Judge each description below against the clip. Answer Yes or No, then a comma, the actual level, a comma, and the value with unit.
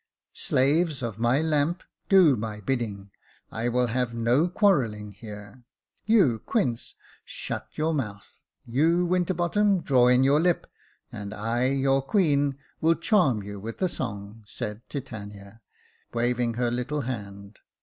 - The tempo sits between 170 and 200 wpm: No, average, 140 wpm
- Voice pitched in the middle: No, low, 125 Hz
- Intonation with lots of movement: Yes, wide, 5.9 semitones